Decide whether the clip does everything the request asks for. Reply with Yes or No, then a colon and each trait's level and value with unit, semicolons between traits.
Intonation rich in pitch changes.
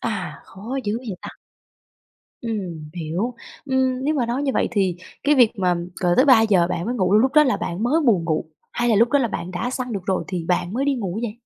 Yes: wide, 5.7 semitones